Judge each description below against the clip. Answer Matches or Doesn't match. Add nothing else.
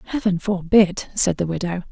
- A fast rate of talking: Doesn't match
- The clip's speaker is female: Matches